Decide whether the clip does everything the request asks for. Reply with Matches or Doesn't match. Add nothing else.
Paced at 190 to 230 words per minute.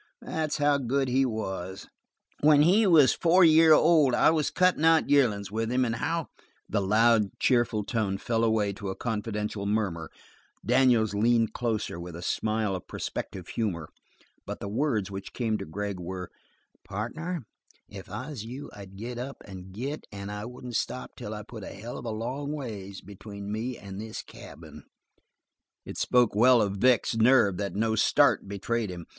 Doesn't match